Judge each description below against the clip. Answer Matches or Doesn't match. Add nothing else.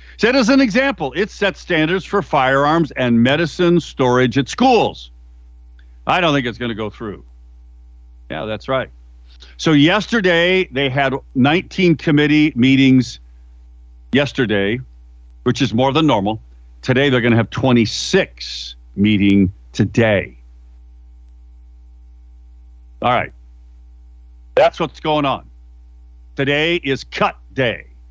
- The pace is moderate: Doesn't match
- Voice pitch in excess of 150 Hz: Doesn't match